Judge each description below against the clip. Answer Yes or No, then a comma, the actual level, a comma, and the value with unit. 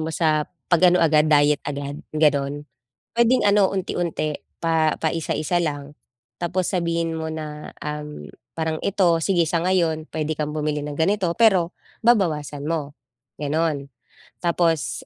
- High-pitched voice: No, medium, 160 Hz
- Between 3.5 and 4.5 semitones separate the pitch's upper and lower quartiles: No, narrow, 2.5 semitones